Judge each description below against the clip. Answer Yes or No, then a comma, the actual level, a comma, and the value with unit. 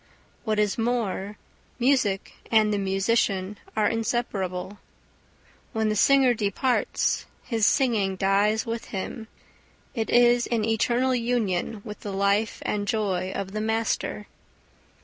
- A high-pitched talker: Yes, high, 215 Hz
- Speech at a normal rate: No, slow, 125 wpm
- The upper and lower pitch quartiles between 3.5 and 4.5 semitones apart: No, average, 2.9 semitones